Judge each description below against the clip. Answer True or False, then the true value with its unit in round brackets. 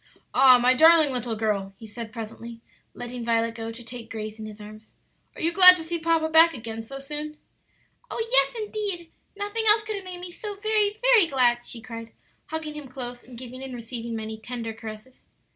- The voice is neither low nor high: False (255 Hz)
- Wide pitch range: True (6.7 semitones)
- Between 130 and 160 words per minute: False (200 wpm)